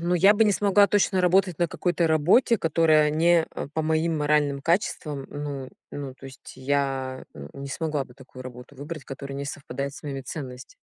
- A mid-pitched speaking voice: Yes, medium, 150 Hz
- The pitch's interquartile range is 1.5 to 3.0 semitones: No, average, 3.7 semitones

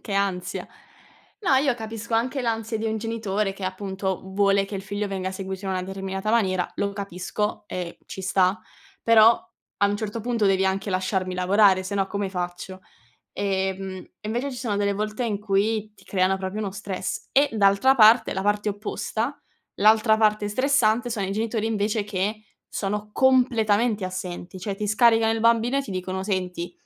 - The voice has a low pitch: No, high, 205 Hz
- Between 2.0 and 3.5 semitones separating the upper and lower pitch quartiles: Yes, narrow, 2.6 semitones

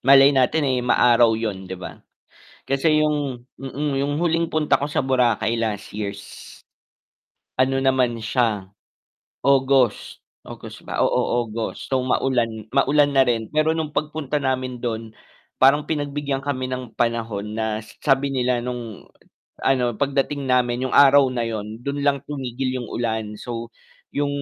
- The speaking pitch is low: Yes, low, 130 Hz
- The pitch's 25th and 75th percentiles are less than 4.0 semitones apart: Yes, average, 3.2 semitones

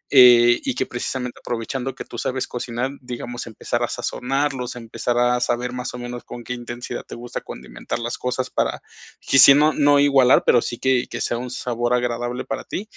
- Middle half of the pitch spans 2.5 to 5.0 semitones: No, narrow, 1.2 semitones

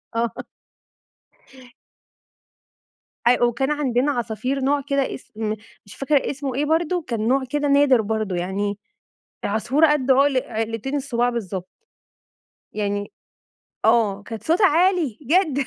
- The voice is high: Yes, very high, 255 Hz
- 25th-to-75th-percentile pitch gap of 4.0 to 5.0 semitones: Yes, average, 4.6 semitones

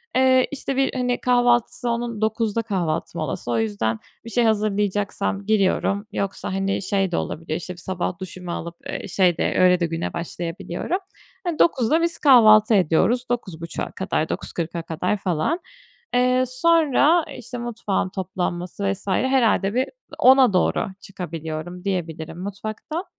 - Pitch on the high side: Yes, high, 200 Hz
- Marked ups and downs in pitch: Yes, wide, 5.7 semitones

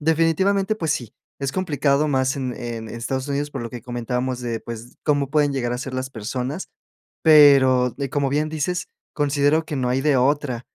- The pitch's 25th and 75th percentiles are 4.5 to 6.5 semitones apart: No, average, 3.1 semitones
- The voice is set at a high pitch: No, low, 135 Hz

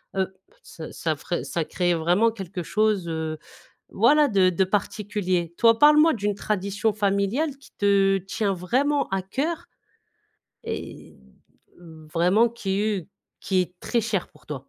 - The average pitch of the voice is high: Yes, high, 195 Hz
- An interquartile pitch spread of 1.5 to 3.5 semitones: No, average, 3.9 semitones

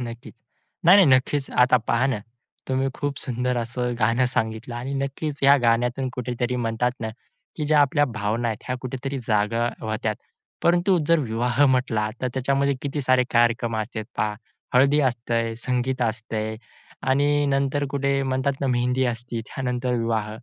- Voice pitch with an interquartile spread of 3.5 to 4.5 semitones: No, average, 2.8 semitones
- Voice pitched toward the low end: Yes, low, 125 Hz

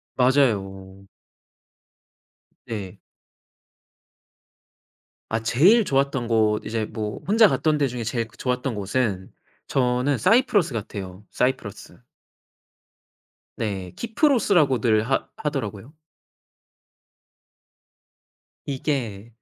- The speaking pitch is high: No, low, 120 Hz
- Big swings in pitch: No, average, 4.9 semitones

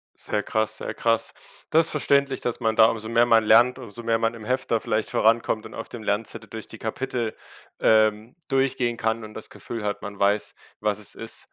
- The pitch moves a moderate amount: No, narrow, 1.6 semitones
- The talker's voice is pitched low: Yes, low, 115 Hz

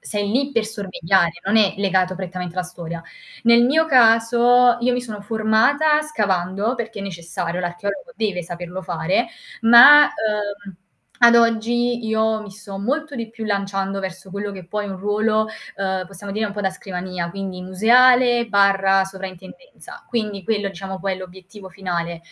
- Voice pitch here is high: Yes, high, 200 Hz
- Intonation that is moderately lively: Yes, average, 3.5 semitones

